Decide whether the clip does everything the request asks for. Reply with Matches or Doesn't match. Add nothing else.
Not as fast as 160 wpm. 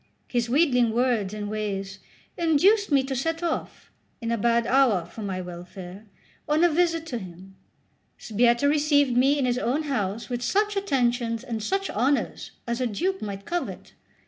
Doesn't match